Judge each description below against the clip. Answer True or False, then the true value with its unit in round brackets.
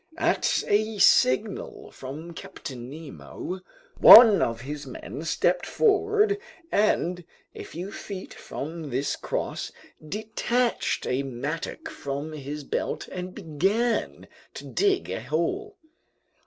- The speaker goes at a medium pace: False (115 wpm)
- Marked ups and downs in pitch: True (7.8 semitones)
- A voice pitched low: False (175 Hz)